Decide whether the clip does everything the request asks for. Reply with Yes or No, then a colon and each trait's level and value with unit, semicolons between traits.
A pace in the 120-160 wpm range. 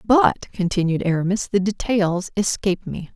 Yes: slow, 135 wpm